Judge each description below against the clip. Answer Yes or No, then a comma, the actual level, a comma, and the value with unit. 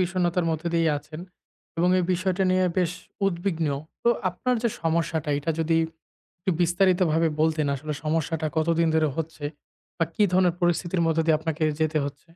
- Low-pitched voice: No, medium, 165 Hz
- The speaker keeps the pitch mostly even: Yes, narrow, 2.1 semitones